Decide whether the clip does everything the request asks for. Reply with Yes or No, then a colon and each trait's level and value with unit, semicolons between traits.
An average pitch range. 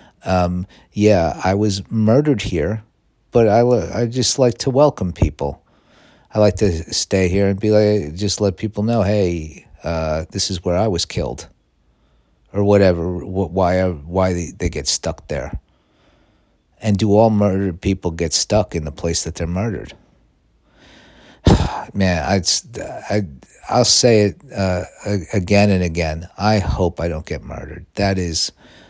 Yes: average, 3.6 semitones